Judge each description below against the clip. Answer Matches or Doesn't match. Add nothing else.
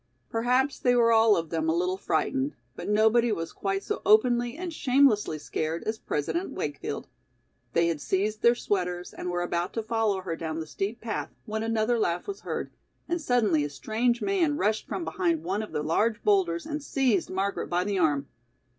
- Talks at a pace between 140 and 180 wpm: Doesn't match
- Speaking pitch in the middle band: Doesn't match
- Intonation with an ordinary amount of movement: Doesn't match